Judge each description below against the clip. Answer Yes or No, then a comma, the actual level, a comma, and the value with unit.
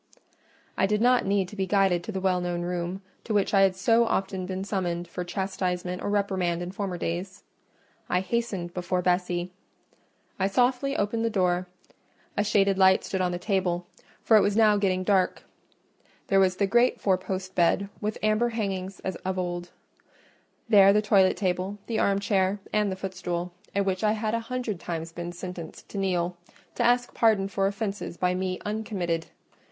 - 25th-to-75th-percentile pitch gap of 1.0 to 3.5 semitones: Yes, narrow, 2.4 semitones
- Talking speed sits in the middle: Yes, average, 180 wpm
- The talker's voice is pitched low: No, high, 190 Hz